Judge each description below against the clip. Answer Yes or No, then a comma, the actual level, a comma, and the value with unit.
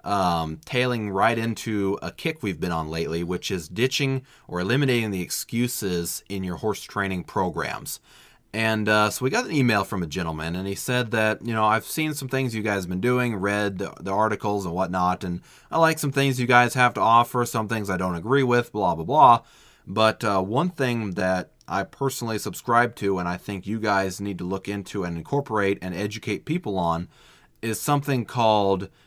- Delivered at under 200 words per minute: No, fast, 205 wpm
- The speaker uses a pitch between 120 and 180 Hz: No, low, 105 Hz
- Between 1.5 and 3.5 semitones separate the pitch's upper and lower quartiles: No, average, 4.4 semitones